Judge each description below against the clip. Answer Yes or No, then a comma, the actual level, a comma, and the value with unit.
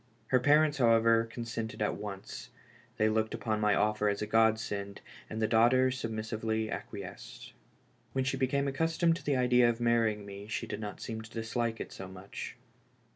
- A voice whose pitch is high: No, low, 115 Hz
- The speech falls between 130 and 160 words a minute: No, average, 180 wpm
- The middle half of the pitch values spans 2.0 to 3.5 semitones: Yes, narrow, 2.6 semitones